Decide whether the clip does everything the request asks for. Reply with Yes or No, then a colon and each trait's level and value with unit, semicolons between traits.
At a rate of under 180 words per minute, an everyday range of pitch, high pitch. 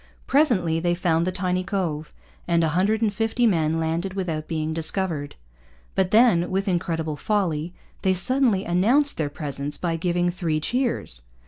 No: average, 155 wpm; average, 3.4 semitones; medium, 175 Hz